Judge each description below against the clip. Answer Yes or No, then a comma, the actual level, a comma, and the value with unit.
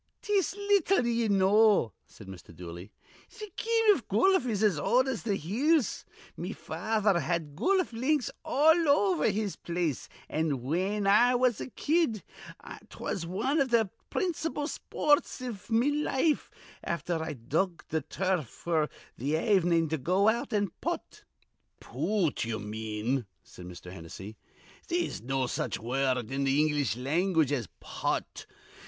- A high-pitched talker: Yes, high, 195 Hz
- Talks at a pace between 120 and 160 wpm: Yes, average, 145 wpm